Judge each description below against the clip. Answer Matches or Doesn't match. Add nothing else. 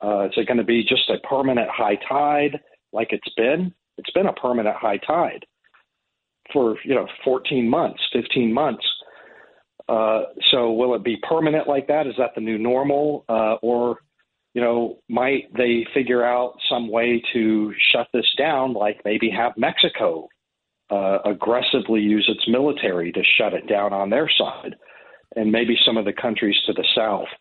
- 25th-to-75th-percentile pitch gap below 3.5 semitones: Matches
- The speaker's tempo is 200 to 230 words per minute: Doesn't match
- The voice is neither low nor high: Doesn't match